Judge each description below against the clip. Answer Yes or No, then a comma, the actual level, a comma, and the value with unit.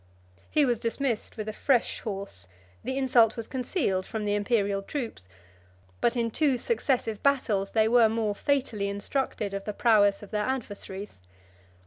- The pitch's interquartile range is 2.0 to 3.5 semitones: No, average, 3.9 semitones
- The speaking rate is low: No, average, 155 wpm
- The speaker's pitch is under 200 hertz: No, high, 220 Hz